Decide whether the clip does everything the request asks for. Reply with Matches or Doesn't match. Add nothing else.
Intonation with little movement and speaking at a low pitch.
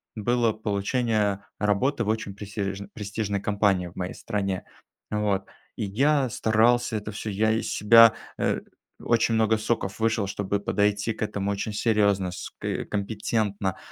Matches